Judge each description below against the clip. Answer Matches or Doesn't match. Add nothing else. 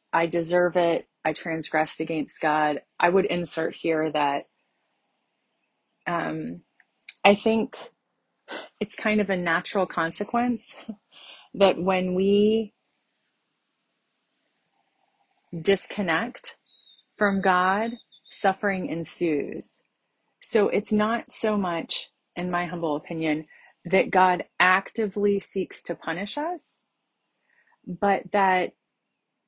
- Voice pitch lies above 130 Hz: Matches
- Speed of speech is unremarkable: Doesn't match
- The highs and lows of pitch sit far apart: Doesn't match